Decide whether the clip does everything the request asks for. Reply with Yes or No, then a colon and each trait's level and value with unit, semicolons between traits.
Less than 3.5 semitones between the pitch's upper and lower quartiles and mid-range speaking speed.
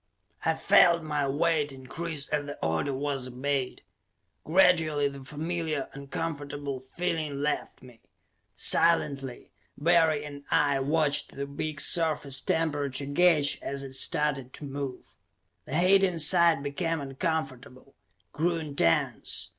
No: average, 2.9 semitones; slow, 120 wpm